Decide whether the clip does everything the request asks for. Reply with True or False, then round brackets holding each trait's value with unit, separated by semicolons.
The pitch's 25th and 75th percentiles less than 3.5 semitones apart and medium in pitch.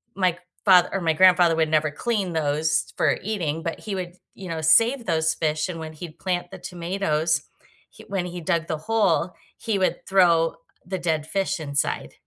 True (2.9 semitones; 170 Hz)